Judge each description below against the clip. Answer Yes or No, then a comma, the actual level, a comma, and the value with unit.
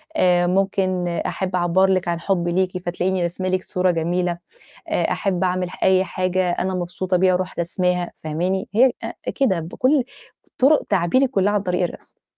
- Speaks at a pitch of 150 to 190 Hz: Yes, medium, 185 Hz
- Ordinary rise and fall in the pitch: No, narrow, 1.3 semitones